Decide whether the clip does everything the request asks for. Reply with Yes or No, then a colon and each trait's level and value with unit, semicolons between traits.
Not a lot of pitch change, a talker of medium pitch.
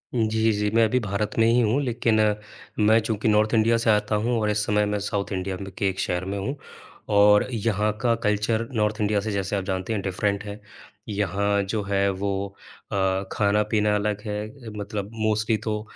No: narrow, 1.5 semitones; low, 105 Hz